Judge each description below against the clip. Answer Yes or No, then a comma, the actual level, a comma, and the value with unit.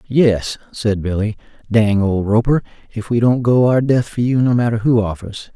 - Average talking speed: Yes, average, 195 wpm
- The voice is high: No, low, 115 Hz